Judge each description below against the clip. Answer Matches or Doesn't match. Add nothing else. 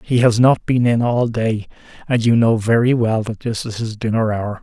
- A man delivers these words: Matches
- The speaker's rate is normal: Doesn't match